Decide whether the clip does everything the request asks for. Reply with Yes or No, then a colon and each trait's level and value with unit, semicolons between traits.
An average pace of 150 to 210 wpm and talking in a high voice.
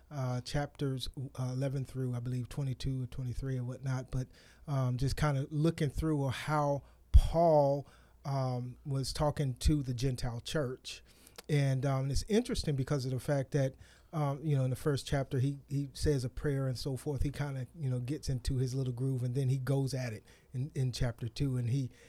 No: average, 200 wpm; low, 135 Hz